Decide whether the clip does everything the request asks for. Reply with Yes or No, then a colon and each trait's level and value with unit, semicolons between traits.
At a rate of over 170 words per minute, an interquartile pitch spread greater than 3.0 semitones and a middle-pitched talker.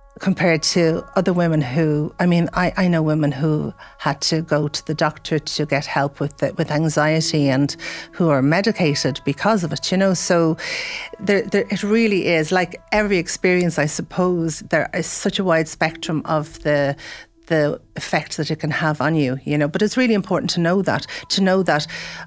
Yes: average, 195 wpm; average, 3.7 semitones; medium, 165 Hz